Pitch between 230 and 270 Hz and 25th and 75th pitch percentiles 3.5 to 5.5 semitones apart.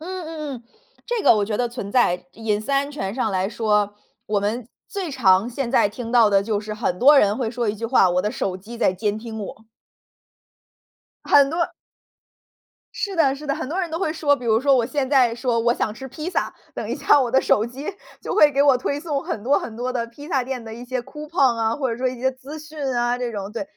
Yes: high, 245 Hz; average, 4.5 semitones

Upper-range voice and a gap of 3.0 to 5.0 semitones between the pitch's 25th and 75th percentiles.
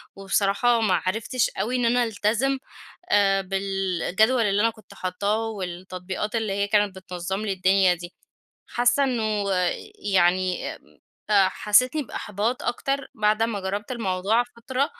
Yes: high, 205 Hz; average, 3.3 semitones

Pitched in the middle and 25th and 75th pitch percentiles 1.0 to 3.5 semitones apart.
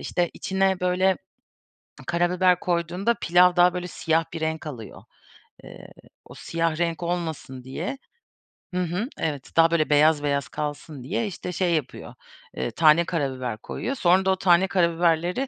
Yes: medium, 170 Hz; average, 2.7 semitones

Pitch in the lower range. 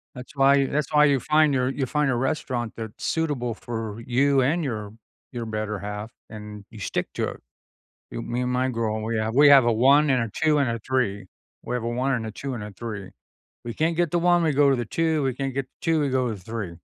Yes: low, 125 Hz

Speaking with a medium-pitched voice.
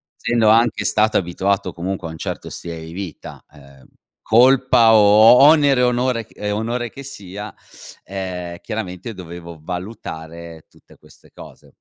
No: low, 100 Hz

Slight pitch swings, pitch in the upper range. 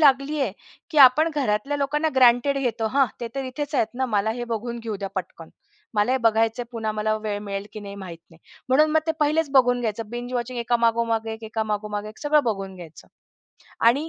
No: average, 4.1 semitones; high, 235 Hz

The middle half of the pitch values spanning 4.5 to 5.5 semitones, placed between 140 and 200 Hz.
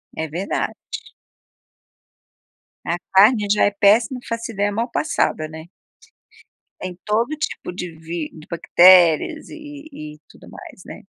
Yes: average, 5.2 semitones; high, 195 Hz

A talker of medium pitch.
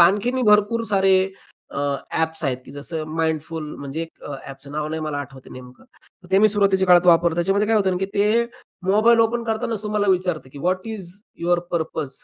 Yes: medium, 180 Hz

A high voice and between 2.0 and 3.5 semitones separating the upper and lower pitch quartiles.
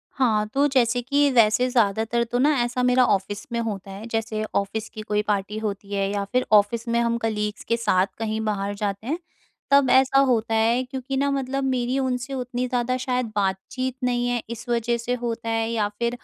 Yes: high, 235 Hz; average, 2.9 semitones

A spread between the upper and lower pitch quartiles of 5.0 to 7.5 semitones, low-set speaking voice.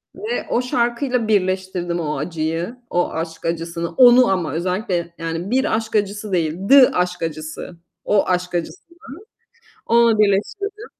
No: wide, 5.6 semitones; medium, 185 Hz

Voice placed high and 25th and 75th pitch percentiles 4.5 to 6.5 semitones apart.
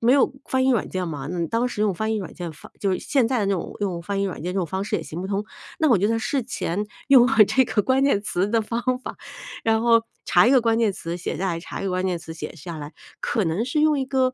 Yes: high, 205 Hz; average, 5.2 semitones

